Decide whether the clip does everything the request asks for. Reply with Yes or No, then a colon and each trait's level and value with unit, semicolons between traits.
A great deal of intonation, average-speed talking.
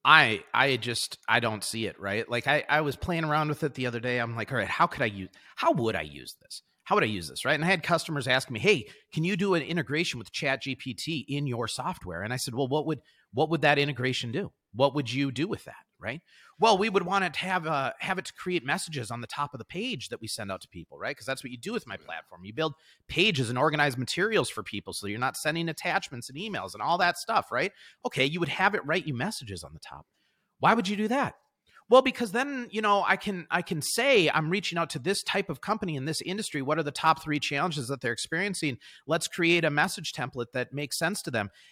No: wide, 5.9 semitones; fast, 265 wpm